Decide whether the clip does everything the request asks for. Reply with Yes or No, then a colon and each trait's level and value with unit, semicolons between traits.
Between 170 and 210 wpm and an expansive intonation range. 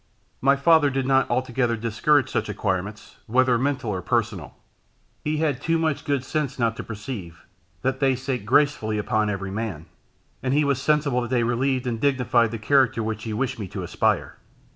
No: average, 185 wpm; average, 4.1 semitones